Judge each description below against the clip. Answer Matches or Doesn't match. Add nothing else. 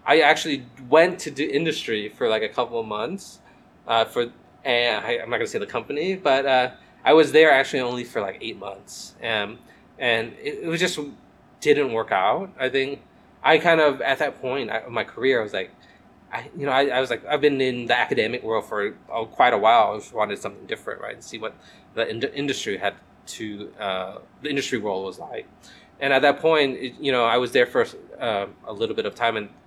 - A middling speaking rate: Doesn't match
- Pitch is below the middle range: Doesn't match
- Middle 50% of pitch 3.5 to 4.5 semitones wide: Doesn't match